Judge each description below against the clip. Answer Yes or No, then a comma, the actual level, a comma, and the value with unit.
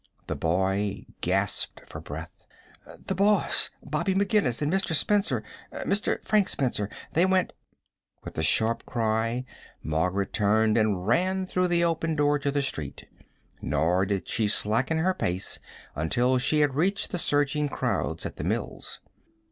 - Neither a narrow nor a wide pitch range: No, wide, 8.9 semitones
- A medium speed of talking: Yes, average, 150 wpm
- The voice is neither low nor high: No, low, 130 Hz